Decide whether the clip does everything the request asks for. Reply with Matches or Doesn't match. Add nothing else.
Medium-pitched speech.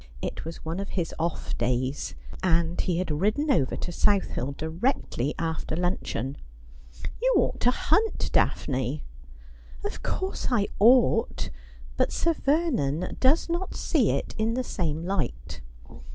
Matches